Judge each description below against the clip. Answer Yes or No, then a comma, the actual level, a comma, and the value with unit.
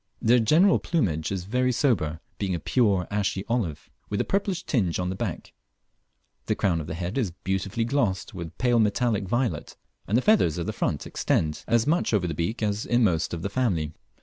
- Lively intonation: Yes, wide, 5.7 semitones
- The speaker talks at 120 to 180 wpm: No, average, 200 wpm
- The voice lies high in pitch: No, low, 100 Hz